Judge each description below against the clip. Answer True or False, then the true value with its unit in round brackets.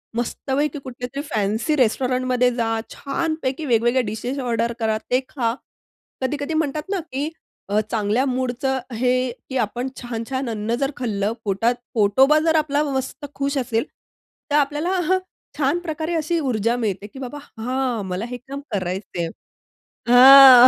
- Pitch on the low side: False (255 Hz)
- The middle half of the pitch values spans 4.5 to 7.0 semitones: False (3.7 semitones)